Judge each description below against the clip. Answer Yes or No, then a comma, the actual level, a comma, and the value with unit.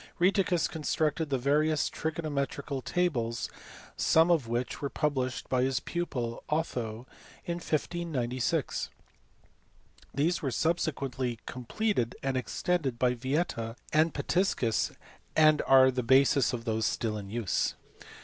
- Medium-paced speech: No, slow, 115 wpm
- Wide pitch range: No, average, 4.6 semitones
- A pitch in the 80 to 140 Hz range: Yes, low, 135 Hz